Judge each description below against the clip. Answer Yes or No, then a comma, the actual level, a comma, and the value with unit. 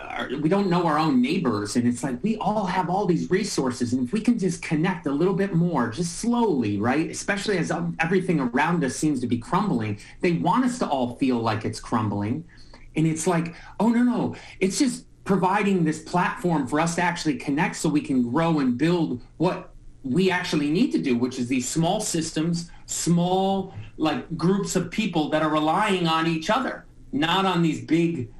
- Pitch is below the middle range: No, medium, 170 Hz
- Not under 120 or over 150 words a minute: No, average, 200 wpm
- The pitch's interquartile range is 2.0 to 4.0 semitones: No, average, 4.6 semitones